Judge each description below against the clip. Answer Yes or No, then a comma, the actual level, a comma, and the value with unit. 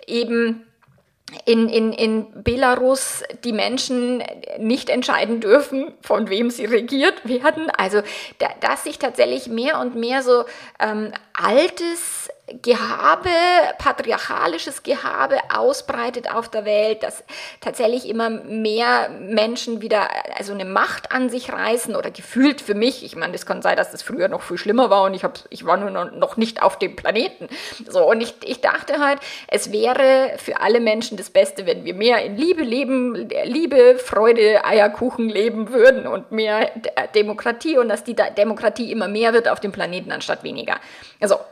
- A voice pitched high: Yes, high, 235 Hz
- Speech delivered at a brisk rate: No, average, 160 wpm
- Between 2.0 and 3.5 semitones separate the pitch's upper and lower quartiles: No, average, 4.0 semitones